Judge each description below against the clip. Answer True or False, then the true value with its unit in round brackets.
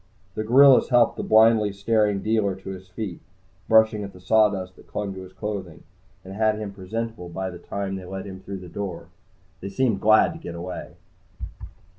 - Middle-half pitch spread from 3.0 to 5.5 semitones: False (2.6 semitones)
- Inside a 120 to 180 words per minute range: False (190 wpm)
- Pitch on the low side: True (100 Hz)